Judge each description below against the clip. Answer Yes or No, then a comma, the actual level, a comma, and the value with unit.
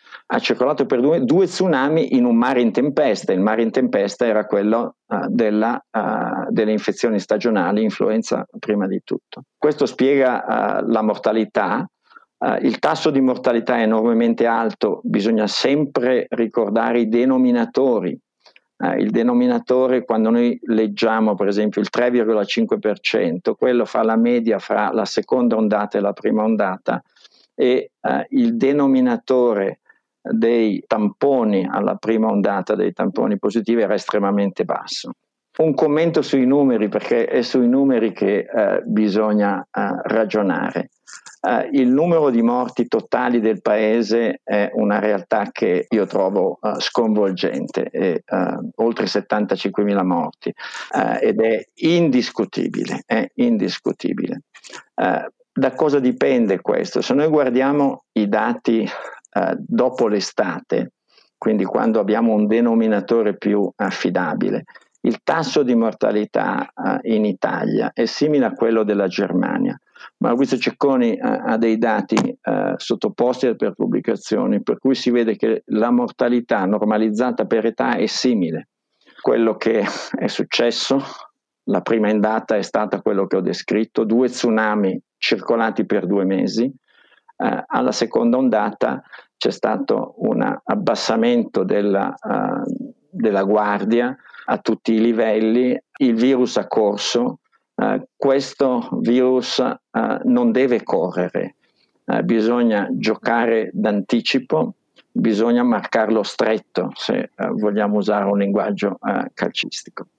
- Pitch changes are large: No, average, 4.0 semitones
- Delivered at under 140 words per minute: Yes, average, 125 wpm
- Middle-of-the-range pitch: No, low, 115 Hz